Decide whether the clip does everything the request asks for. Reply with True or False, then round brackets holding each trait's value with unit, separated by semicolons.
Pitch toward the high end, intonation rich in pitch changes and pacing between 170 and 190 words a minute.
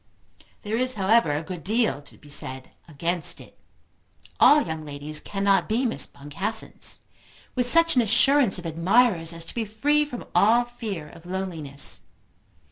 False (195 Hz; 6.9 semitones; 155 wpm)